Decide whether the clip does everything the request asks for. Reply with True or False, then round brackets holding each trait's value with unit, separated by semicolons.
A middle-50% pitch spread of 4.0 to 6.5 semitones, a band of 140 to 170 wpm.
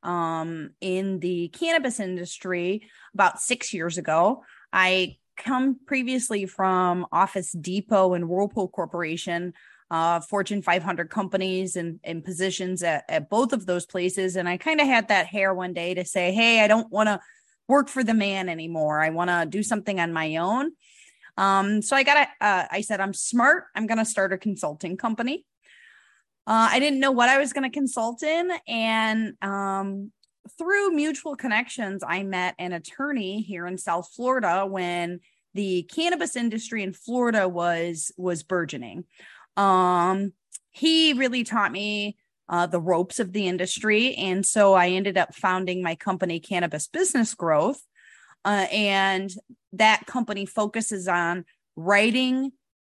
True (4.5 semitones; 155 wpm)